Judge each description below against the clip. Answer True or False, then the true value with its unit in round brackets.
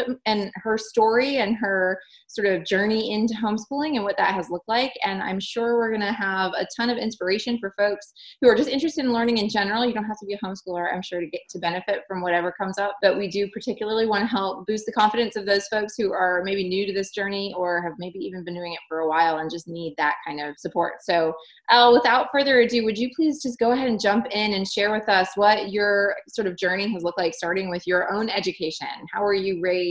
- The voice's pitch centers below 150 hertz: False (200 Hz)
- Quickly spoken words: True (255 wpm)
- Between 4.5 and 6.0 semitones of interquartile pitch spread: False (3.5 semitones)